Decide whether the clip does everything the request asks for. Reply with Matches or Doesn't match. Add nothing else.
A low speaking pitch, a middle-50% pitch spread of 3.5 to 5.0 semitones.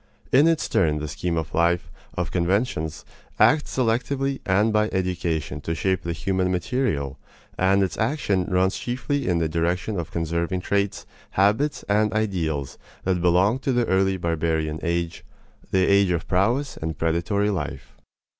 Matches